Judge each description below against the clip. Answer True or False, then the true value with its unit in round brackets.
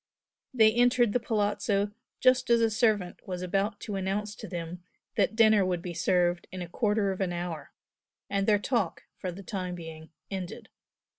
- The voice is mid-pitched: False (195 Hz)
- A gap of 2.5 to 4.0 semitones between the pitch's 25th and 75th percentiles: True (3.4 semitones)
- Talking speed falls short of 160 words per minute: False (175 wpm)